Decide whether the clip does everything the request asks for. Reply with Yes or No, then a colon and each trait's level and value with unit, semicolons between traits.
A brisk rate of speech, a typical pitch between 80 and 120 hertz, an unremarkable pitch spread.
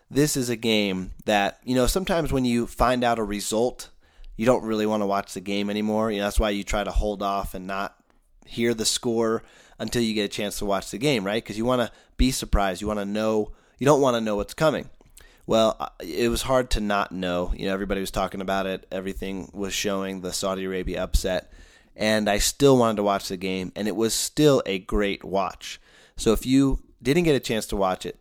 Yes: fast, 235 wpm; low, 105 Hz; average, 3.1 semitones